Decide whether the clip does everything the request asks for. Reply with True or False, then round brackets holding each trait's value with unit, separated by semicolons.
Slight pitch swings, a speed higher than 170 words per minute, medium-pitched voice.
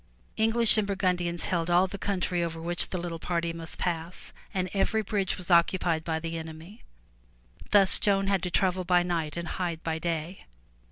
True (2.3 semitones; 185 wpm; 175 Hz)